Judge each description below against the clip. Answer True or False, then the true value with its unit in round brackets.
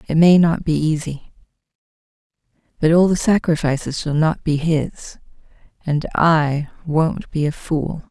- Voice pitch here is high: False (155 Hz)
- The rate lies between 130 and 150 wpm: True (140 wpm)